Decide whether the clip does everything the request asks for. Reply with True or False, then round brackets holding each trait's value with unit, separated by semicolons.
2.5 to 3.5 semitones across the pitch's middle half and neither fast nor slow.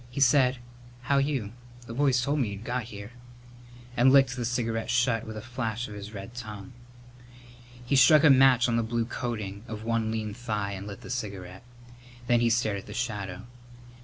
True (2.9 semitones; 190 wpm)